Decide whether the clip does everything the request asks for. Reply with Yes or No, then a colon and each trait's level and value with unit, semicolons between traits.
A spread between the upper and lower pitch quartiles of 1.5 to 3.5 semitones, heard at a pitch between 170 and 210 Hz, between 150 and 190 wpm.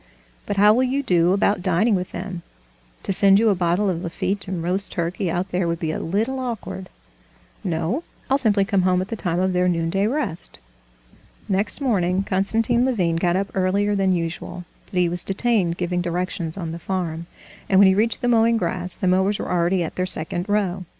No: average, 2.7 semitones; medium, 185 Hz; fast, 205 wpm